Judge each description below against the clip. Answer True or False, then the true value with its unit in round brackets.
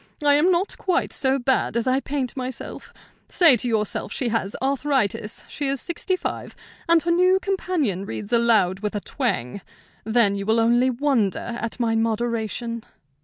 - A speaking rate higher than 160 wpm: True (170 wpm)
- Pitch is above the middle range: True (240 Hz)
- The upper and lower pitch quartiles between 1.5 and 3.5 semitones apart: False (4.5 semitones)